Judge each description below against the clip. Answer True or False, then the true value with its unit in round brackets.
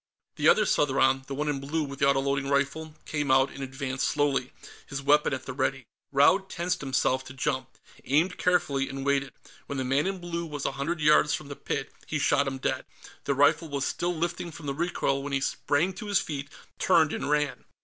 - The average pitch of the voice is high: False (140 Hz)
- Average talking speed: False (210 wpm)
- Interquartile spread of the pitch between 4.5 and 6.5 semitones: False (2.4 semitones)